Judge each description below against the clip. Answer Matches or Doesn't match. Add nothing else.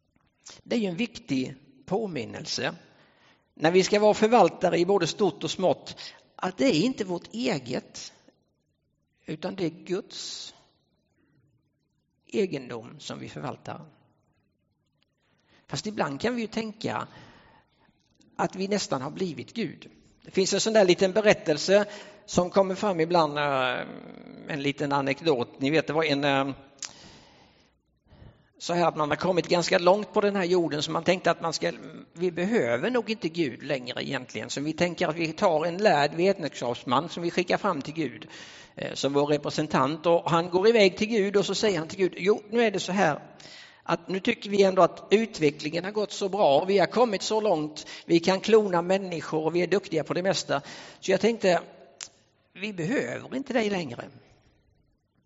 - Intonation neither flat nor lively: Matches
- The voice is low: Doesn't match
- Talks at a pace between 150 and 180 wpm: Matches